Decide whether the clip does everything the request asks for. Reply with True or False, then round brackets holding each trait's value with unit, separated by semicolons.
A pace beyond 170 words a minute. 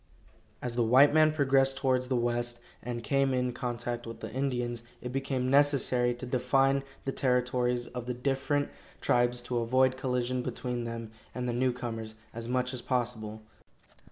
False (160 wpm)